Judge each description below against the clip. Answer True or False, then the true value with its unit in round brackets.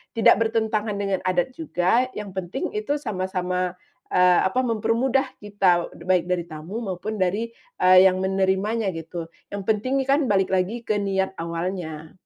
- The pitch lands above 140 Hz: True (190 Hz)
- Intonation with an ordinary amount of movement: True (3.3 semitones)